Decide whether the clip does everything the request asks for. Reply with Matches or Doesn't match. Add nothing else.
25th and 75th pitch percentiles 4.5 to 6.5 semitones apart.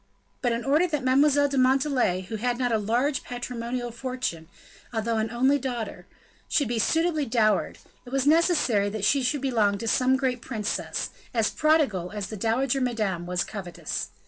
Doesn't match